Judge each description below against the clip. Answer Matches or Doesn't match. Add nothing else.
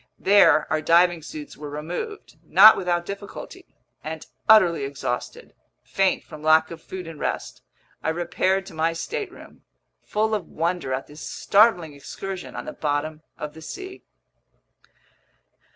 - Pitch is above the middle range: Doesn't match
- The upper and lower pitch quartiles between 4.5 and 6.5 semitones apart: Doesn't match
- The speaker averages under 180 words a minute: Matches